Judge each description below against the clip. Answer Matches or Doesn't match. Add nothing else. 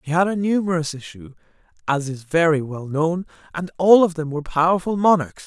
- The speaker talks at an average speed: Matches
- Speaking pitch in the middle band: Matches